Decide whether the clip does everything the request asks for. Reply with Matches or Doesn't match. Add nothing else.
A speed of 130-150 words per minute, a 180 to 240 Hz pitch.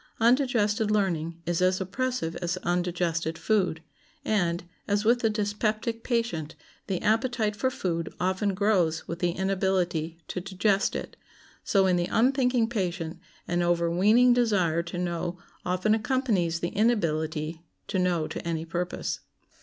Matches